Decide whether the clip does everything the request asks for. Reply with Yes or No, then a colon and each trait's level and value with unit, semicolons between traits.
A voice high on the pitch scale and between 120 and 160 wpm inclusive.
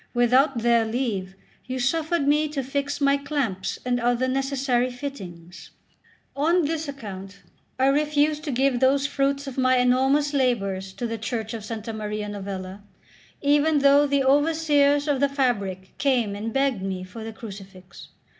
Yes: very high, 255 Hz; average, 155 wpm